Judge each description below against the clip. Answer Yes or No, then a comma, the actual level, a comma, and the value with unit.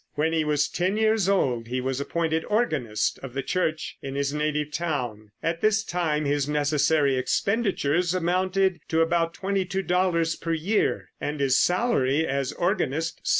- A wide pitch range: No, average, 4.5 semitones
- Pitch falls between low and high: Yes, medium, 160 Hz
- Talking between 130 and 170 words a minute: Yes, average, 155 wpm